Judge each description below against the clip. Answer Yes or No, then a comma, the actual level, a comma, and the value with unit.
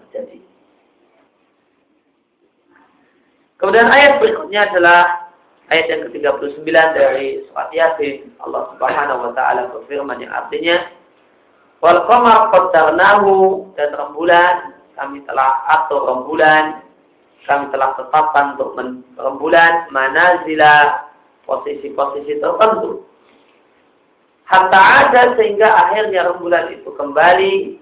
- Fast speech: No, average, 90 wpm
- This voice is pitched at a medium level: Yes, medium, 175 Hz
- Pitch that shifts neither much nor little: No, wide, 6.7 semitones